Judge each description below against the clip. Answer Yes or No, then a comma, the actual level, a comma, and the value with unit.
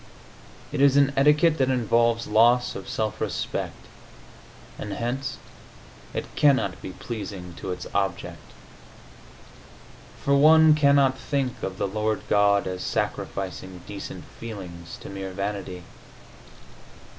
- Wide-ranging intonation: Yes, wide, 5.9 semitones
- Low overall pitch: Yes, low, 110 Hz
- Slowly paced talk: Yes, slow, 120 wpm